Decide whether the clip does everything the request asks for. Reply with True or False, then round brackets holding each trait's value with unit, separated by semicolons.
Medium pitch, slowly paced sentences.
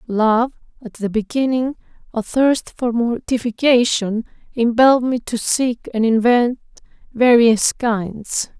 False (235 Hz; 105 wpm)